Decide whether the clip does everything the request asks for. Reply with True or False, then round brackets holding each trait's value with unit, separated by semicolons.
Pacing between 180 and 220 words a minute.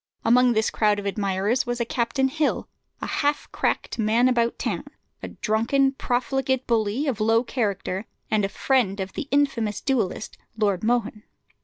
False (160 wpm)